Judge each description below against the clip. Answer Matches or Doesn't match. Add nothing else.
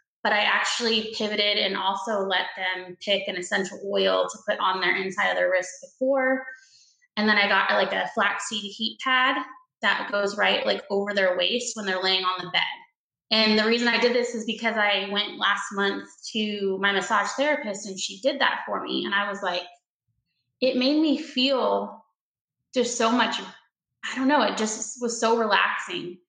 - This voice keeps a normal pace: Matches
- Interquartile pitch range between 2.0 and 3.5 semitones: Doesn't match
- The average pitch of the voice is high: Matches